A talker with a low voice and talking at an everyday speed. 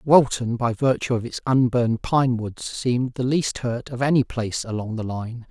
Yes: low, 120 Hz; average, 195 wpm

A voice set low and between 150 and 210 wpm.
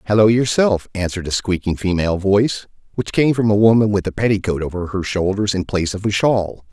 Yes: low, 100 Hz; fast, 205 wpm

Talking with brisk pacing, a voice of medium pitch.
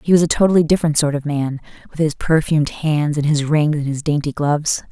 Yes: fast, 230 wpm; medium, 150 Hz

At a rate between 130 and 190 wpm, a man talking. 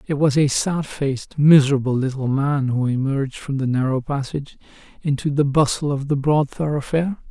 Yes: average, 170 wpm; male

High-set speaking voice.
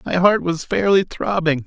No: medium, 170 Hz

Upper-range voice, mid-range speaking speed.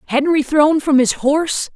Yes: very high, 290 Hz; average, 170 wpm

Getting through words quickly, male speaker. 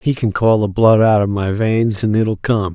Yes: fast, 260 wpm; male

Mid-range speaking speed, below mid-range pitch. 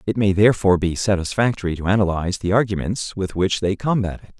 Yes: average, 190 wpm; low, 100 Hz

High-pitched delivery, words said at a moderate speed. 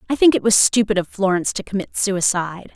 No: high, 200 Hz; fast, 215 wpm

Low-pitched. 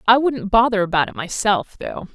No: high, 210 Hz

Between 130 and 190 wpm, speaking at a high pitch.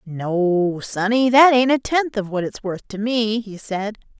No: average, 200 wpm; high, 215 Hz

